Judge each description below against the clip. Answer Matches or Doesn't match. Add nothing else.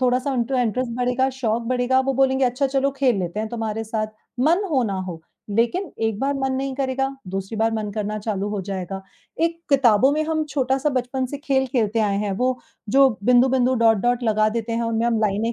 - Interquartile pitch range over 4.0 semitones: Doesn't match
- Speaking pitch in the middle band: Doesn't match